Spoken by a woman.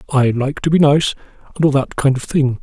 No: male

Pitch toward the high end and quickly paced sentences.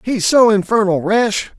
No: high, 210 Hz; average, 150 wpm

